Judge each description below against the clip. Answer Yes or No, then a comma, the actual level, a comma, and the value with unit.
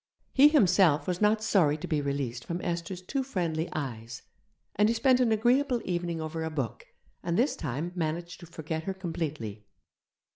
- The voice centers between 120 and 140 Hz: No, medium, 170 Hz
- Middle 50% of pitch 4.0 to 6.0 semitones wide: Yes, average, 5.1 semitones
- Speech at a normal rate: Yes, average, 175 wpm